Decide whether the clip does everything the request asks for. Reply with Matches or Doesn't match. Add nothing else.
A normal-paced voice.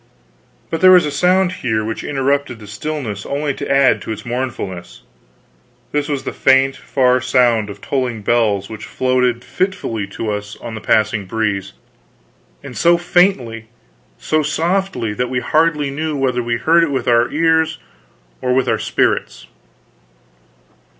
Matches